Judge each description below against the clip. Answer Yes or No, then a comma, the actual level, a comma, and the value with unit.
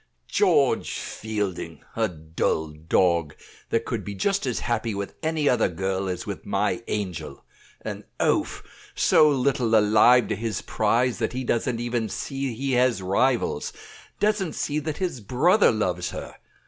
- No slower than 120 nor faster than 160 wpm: Yes, average, 150 wpm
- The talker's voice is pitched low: Yes, low, 115 Hz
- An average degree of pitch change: No, wide, 5.7 semitones